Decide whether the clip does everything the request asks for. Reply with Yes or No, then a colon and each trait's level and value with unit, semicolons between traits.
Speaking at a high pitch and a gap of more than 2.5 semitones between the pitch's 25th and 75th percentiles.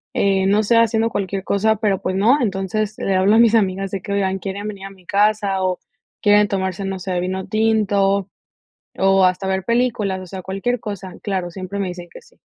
No: high, 195 Hz; narrow, 1.9 semitones